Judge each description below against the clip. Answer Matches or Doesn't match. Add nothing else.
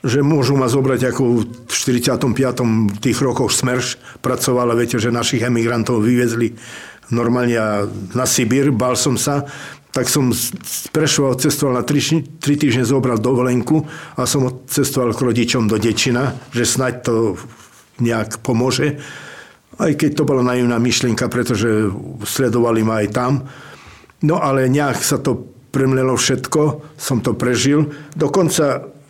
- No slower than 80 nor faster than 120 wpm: Doesn't match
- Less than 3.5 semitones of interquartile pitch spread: Matches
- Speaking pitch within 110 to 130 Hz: Matches